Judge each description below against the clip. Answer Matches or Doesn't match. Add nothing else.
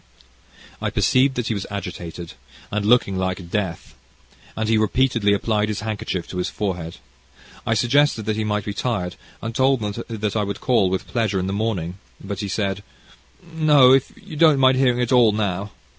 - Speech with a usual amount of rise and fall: Matches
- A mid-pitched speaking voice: Doesn't match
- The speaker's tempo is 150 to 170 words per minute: Doesn't match